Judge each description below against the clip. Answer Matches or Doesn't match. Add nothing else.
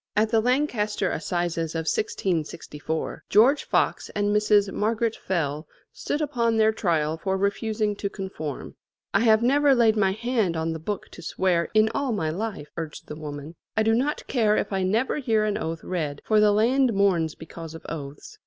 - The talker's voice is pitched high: Matches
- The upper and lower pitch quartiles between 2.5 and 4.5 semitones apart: Doesn't match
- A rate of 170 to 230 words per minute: Matches